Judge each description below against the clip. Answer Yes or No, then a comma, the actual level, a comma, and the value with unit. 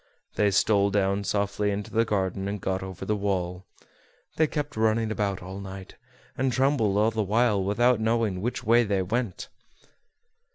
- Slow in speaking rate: No, average, 165 wpm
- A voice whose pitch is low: Yes, low, 105 Hz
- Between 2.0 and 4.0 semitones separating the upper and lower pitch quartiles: Yes, average, 2.7 semitones